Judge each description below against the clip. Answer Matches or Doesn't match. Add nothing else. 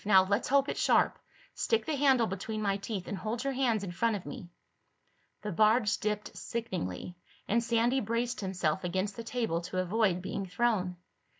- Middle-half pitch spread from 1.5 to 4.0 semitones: Matches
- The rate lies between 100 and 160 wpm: Doesn't match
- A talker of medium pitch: Doesn't match